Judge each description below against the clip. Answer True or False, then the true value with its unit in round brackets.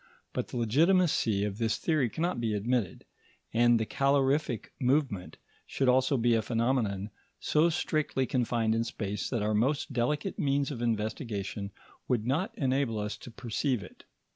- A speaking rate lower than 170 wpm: True (155 wpm)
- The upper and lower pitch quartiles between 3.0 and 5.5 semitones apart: True (3.9 semitones)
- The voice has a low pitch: True (120 Hz)